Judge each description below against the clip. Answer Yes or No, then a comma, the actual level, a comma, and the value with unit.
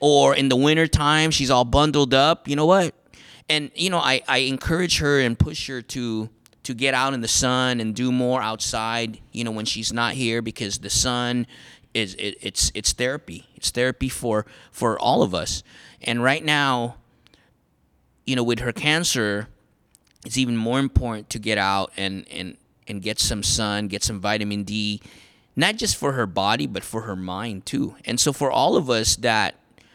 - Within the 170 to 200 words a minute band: Yes, average, 190 wpm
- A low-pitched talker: Yes, low, 120 Hz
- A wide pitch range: No, average, 3.8 semitones